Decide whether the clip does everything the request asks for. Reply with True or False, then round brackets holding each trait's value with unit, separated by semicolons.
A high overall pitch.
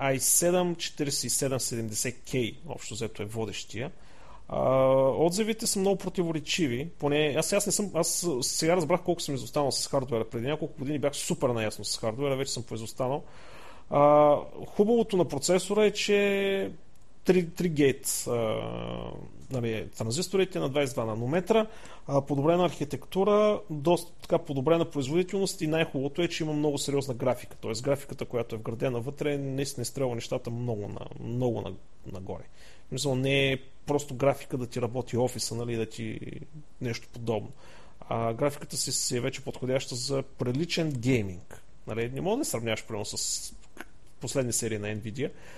False (140 Hz)